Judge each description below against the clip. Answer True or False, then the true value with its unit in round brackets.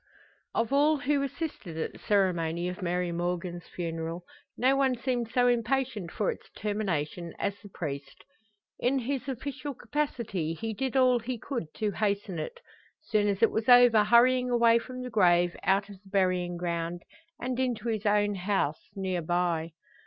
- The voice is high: True (205 Hz)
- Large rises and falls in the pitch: True (5.9 semitones)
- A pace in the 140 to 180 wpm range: True (165 wpm)